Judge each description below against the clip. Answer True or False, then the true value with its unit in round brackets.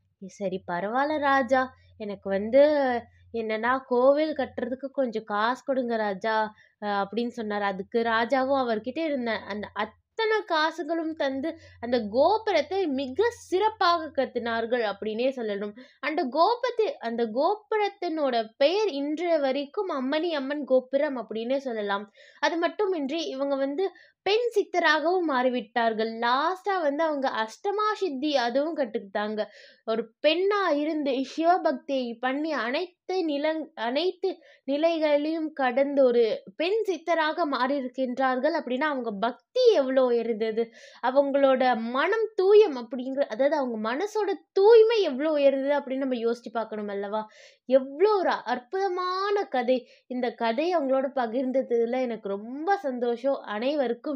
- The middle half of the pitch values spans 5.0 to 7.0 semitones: True (5.4 semitones)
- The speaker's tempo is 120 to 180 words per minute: False (110 wpm)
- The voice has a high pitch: True (275 Hz)